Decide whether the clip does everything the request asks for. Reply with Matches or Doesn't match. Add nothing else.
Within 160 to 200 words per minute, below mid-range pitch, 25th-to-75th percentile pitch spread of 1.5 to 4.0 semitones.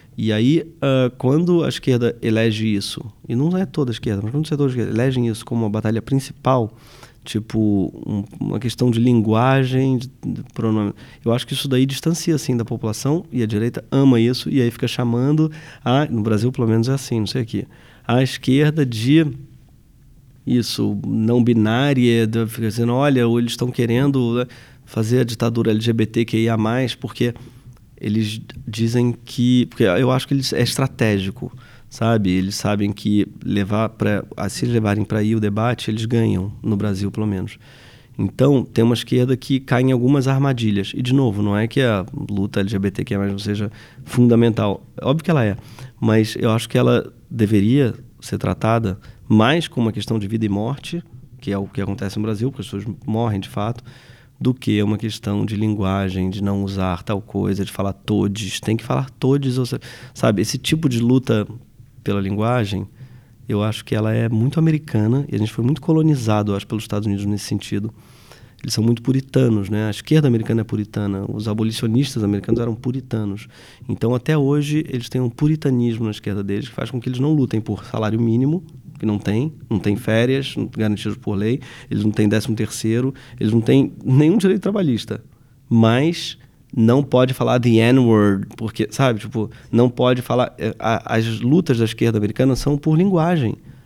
Matches